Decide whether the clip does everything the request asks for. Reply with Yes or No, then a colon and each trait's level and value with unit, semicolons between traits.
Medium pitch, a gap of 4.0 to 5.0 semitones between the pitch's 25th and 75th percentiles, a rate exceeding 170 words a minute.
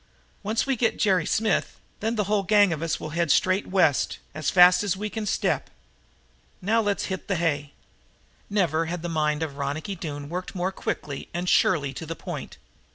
Yes: medium, 180 Hz; average, 4.5 semitones; average, 190 wpm